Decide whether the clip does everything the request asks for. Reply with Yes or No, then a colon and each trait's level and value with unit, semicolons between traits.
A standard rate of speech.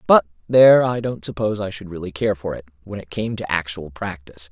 No: fast, 225 wpm